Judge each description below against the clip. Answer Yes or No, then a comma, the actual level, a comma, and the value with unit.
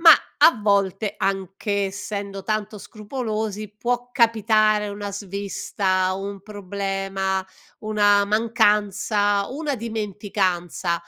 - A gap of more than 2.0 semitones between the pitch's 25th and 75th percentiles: No, narrow, 1.7 semitones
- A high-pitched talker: Yes, high, 205 Hz